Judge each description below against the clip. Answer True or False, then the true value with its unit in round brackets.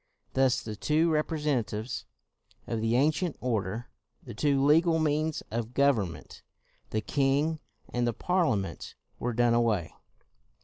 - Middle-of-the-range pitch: False (130 Hz)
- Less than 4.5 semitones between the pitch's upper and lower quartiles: False (5.2 semitones)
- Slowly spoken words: True (125 wpm)